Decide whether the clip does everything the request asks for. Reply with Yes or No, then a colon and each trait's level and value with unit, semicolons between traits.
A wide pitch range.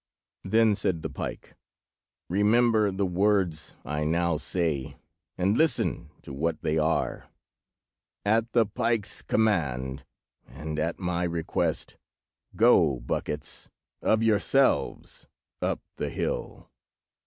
Yes: wide, 5.8 semitones